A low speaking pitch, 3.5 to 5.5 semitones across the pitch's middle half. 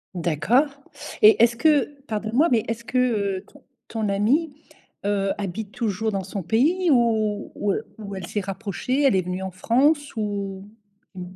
No: high, 215 Hz; average, 4.3 semitones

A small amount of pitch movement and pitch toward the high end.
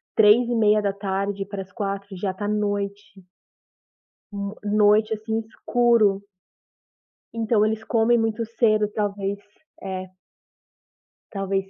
Yes: narrow, 1.8 semitones; high, 205 Hz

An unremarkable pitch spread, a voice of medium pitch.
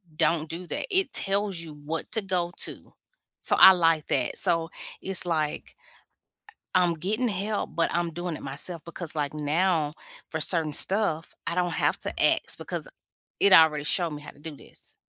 Yes: average, 3.1 semitones; medium, 170 Hz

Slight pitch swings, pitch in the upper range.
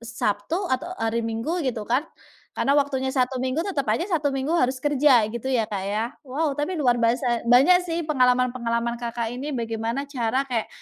No: average, 3.6 semitones; very high, 255 Hz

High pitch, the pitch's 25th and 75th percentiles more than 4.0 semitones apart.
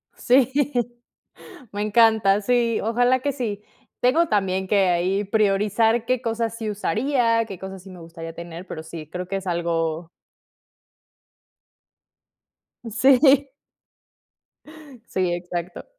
Yes: high, 205 Hz; average, 4.7 semitones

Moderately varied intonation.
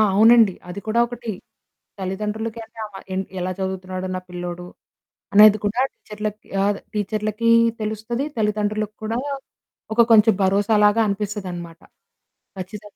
No: narrow, 2.3 semitones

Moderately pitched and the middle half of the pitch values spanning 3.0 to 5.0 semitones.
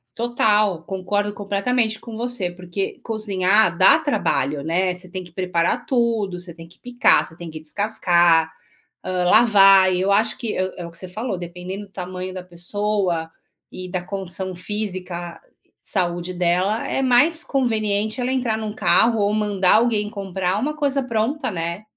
No: high, 195 Hz; average, 3.5 semitones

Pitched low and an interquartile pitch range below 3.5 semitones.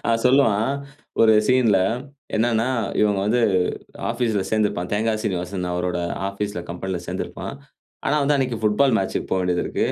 No: low, 105 Hz; average, 3.8 semitones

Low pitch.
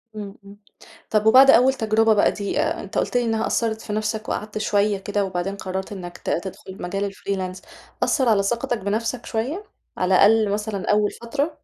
No: high, 210 Hz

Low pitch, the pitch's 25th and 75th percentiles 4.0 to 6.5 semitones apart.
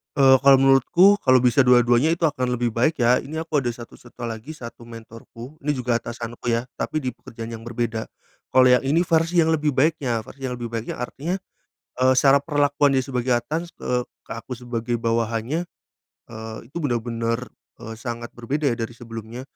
No: low, 125 Hz; average, 3.5 semitones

